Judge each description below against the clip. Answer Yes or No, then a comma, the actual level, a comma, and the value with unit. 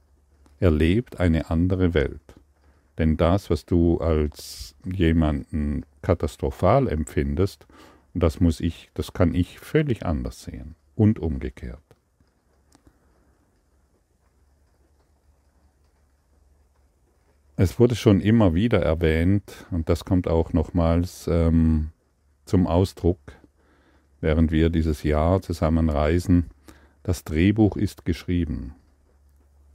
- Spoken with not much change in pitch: No, average, 3.2 semitones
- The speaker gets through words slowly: Yes, slow, 95 wpm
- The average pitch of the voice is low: Yes, very low, 80 Hz